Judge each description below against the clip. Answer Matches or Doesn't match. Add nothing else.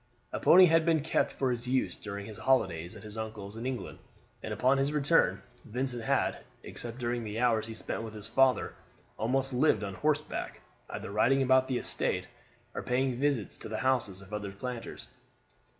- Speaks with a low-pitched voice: Matches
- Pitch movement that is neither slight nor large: Matches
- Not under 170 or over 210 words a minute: Matches